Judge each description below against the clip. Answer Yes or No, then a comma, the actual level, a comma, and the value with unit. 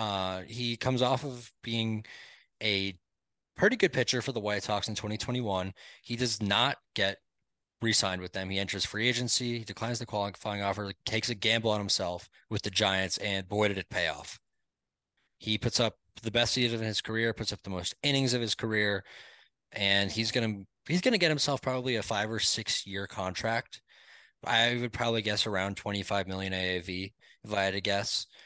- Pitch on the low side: Yes, low, 105 Hz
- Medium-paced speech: Yes, average, 195 wpm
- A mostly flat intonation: No, average, 3.0 semitones